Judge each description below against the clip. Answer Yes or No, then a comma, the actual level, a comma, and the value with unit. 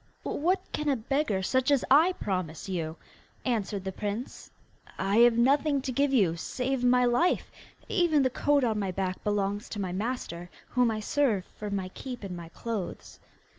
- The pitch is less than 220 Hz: No, high, 230 Hz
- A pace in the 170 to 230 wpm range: Yes, average, 175 wpm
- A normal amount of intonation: No, wide, 5.7 semitones